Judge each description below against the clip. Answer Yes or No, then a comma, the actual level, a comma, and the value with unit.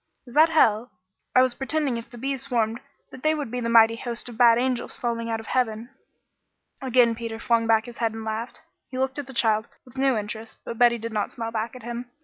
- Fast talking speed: Yes, fast, 235 wpm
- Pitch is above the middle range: Yes, high, 235 Hz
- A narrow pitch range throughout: Yes, narrow, 2.2 semitones